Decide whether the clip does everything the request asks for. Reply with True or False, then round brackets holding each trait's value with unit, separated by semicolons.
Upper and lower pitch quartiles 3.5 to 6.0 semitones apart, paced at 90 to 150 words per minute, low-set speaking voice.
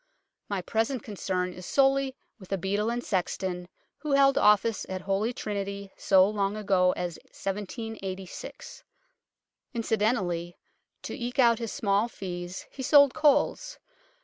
False (4.2 semitones; 135 wpm; 205 Hz)